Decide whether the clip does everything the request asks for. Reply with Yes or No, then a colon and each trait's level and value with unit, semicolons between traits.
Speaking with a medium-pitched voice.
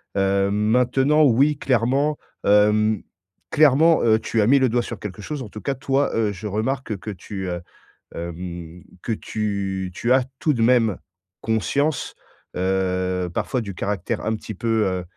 No: low, 110 Hz